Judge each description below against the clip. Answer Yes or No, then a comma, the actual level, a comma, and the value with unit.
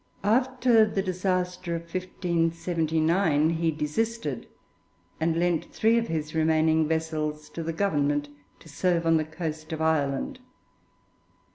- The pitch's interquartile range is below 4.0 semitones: Yes, average, 2.7 semitones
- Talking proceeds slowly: Yes, slow, 125 wpm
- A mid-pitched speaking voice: Yes, medium, 165 Hz